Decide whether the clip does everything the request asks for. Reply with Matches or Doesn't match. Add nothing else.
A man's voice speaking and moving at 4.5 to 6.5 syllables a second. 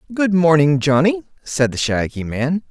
Matches